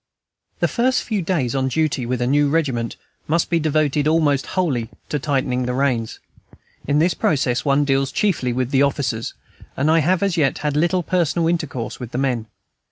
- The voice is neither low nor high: Yes, medium, 145 Hz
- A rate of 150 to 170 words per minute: No, average, 185 wpm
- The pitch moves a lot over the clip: No, average, 4.1 semitones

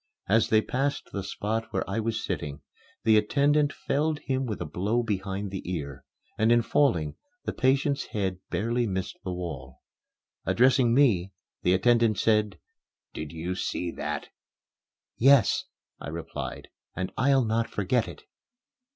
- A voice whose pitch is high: No, low, 110 Hz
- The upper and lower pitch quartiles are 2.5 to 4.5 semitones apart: No, average, 5.2 semitones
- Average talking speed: Yes, average, 145 wpm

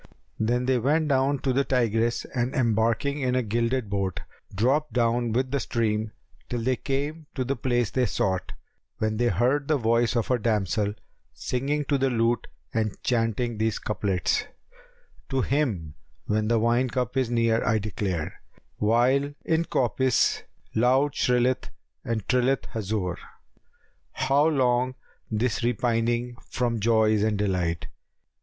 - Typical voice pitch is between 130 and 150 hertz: No, low, 120 Hz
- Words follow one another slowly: No, average, 145 wpm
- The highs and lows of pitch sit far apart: No, average, 3.0 semitones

